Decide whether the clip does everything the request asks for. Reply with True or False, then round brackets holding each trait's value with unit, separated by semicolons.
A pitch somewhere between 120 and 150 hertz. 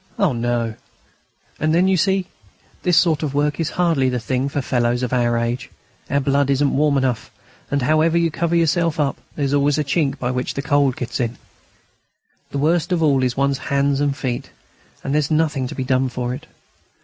True (140 Hz)